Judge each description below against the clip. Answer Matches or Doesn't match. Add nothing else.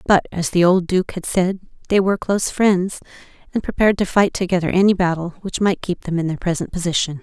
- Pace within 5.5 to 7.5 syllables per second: Matches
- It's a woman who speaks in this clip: Matches